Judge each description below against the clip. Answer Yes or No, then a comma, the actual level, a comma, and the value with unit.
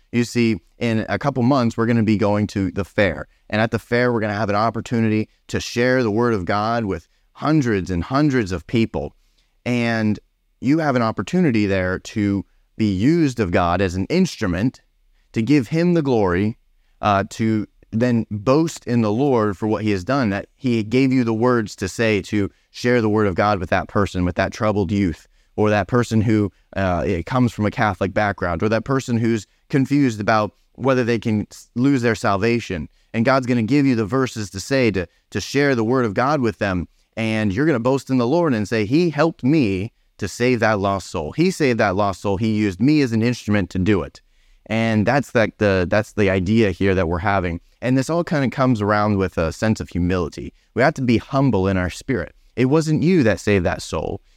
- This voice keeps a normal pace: No, fast, 215 wpm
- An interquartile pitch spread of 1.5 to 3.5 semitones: No, average, 3.9 semitones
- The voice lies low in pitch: Yes, low, 110 Hz